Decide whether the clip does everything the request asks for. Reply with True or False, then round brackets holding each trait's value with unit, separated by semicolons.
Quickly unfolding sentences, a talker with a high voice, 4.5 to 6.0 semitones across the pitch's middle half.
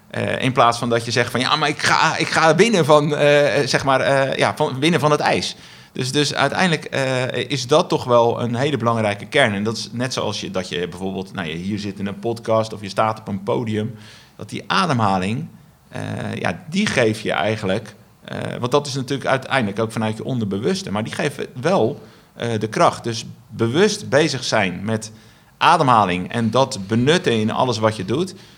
False (205 wpm; 120 Hz; 4.9 semitones)